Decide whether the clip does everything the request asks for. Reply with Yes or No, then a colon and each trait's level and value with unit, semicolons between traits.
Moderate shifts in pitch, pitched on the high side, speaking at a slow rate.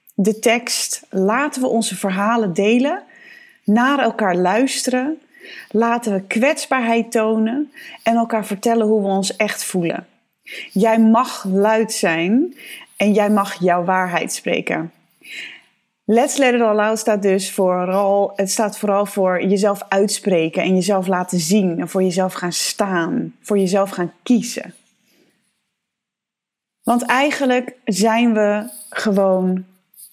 Yes: average, 3.3 semitones; high, 210 Hz; slow, 125 wpm